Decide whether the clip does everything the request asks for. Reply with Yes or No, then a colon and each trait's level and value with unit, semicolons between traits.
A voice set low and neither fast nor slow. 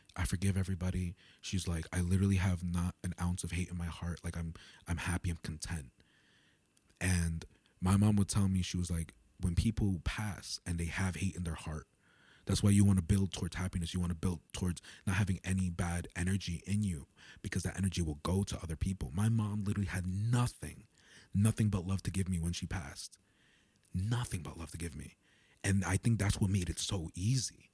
No: very low, 90 Hz; fast, 210 wpm